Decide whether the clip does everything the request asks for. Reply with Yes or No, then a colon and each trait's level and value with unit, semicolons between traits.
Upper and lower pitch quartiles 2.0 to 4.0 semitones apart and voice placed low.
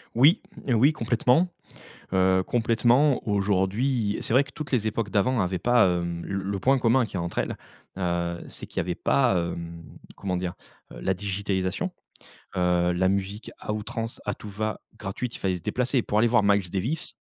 No: average, 4.6 semitones; low, 100 Hz